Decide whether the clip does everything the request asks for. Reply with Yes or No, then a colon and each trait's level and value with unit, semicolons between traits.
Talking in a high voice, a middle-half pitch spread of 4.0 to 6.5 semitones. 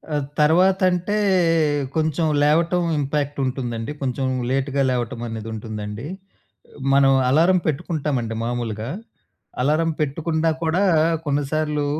No: medium, 145 Hz; average, 4.4 semitones